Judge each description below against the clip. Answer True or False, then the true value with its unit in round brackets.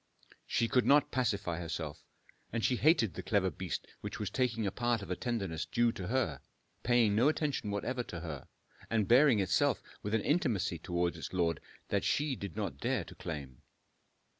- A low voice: True (105 Hz)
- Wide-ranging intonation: True (5.7 semitones)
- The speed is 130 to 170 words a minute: False (185 wpm)